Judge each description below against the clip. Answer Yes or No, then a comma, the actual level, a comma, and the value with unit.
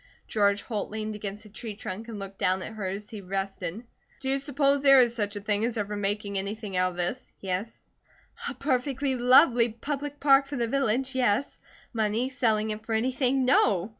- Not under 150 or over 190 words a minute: No, average, 200 wpm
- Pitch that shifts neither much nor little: Yes, average, 4.3 semitones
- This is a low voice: No, high, 220 Hz